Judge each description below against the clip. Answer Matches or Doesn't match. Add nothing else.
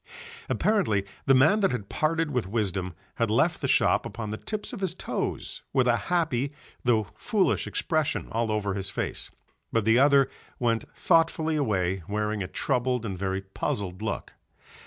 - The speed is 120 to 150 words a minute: Doesn't match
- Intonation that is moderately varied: Doesn't match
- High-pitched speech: Doesn't match